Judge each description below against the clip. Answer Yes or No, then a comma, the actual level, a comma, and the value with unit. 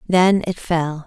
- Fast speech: No, average, 170 wpm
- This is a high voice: No, medium, 170 Hz